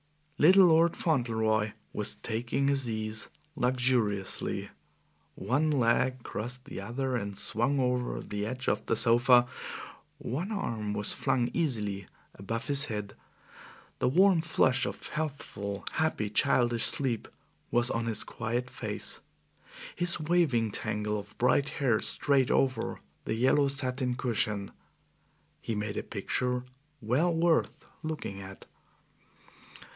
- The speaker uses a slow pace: Yes, slow, 125 wpm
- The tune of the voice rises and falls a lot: No, average, 4.3 semitones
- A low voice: Yes, low, 125 Hz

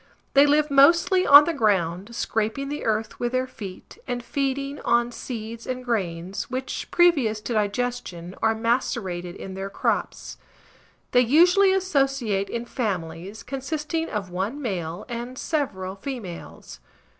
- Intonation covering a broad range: Yes, wide, 5.7 semitones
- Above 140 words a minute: No, slow, 135 wpm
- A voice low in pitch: No, high, 235 Hz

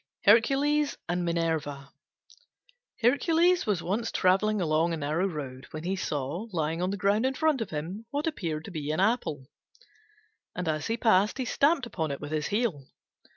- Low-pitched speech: No, medium, 185 Hz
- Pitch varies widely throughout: Yes, wide, 6.8 semitones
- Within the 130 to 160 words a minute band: No, average, 175 wpm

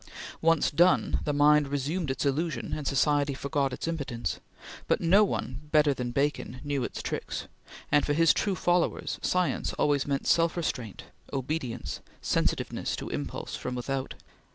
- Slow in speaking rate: No, average, 155 wpm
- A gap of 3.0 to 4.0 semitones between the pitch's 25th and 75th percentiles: Yes, average, 3.3 semitones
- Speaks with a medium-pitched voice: Yes, medium, 145 Hz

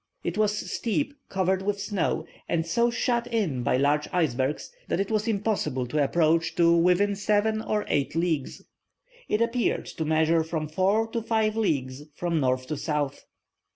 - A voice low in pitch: No, medium, 175 Hz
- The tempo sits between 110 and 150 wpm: No, average, 165 wpm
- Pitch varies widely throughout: Yes, wide, 5.8 semitones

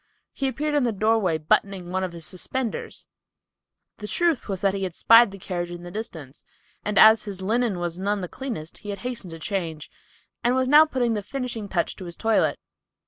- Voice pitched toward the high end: Yes, high, 200 Hz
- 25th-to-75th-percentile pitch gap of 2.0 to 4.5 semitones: No, average, 5.1 semitones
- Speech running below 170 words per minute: No, average, 195 wpm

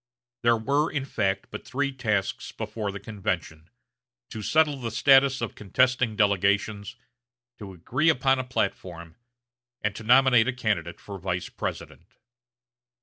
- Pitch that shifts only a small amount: No, average, 4.8 semitones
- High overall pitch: No, low, 110 Hz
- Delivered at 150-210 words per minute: No, average, 140 wpm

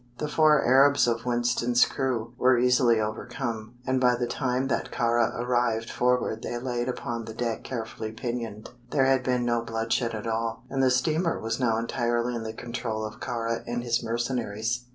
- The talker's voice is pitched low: Yes, low, 120 Hz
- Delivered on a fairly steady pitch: Yes, narrow, 1.6 semitones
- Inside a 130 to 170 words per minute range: No, average, 180 wpm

